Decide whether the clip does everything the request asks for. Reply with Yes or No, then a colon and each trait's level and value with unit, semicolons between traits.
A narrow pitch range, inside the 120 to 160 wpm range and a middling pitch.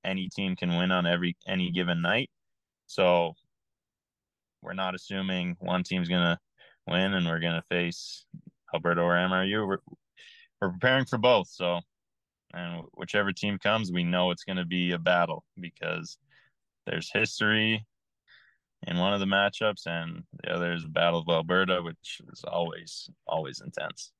No: narrow, 2.2 semitones; average, 155 wpm; very low, 90 Hz